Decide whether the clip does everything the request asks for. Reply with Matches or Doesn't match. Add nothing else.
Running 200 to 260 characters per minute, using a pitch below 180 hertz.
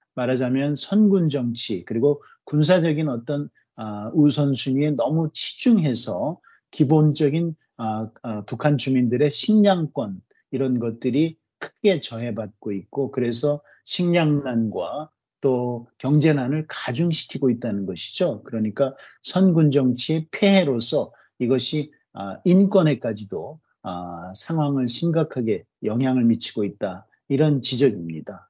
Matches